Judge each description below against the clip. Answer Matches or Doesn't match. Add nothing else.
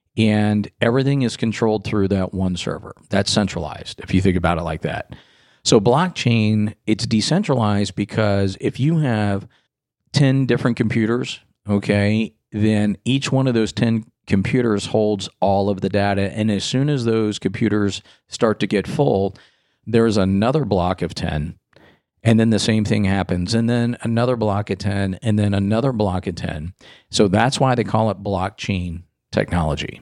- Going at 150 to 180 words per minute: Matches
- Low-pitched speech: Matches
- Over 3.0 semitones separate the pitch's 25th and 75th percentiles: Doesn't match